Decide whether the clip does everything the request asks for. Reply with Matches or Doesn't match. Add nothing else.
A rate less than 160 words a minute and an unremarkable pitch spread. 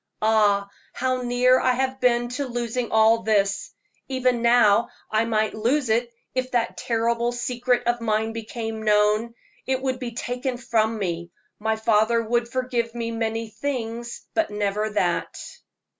Doesn't match